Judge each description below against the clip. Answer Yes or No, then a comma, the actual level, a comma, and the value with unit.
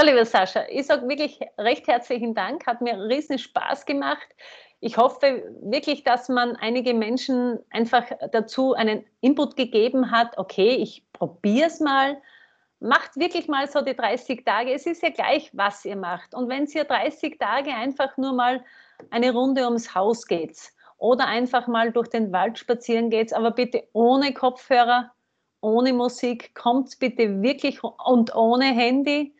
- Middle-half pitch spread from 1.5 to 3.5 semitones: Yes, average, 2.9 semitones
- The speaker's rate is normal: Yes, average, 160 wpm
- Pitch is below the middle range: No, very high, 250 Hz